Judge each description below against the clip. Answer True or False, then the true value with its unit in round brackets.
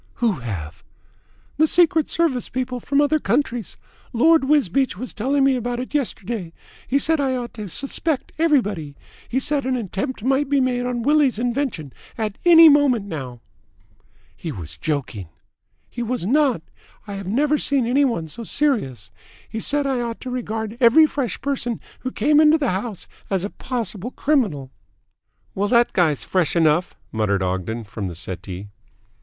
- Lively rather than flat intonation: True (7.6 semitones)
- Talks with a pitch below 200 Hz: False (240 Hz)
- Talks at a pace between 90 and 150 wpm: False (170 wpm)